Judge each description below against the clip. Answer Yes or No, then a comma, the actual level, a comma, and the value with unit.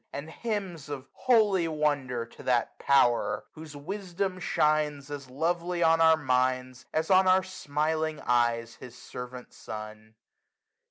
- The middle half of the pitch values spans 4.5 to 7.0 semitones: Yes, average, 5.1 semitones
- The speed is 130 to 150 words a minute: Yes, average, 140 wpm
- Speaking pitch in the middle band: Yes, medium, 150 Hz